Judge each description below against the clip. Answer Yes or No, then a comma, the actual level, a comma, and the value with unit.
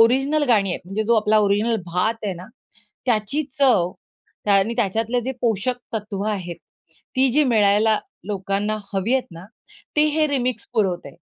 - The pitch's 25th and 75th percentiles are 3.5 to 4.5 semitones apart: Yes, average, 4.0 semitones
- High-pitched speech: Yes, high, 215 Hz